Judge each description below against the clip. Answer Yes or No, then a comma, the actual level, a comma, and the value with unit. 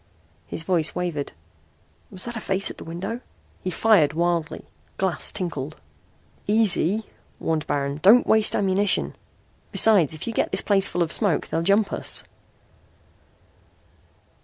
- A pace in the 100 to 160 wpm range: Yes, slow, 135 wpm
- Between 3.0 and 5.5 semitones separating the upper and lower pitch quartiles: Yes, average, 4.1 semitones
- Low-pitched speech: No, medium, 185 Hz